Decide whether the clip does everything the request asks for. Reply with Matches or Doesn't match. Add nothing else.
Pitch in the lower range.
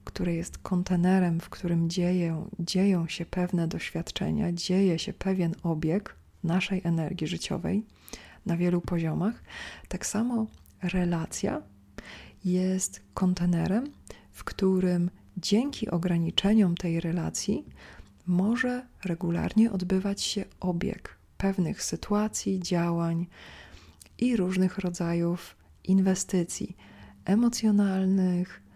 Doesn't match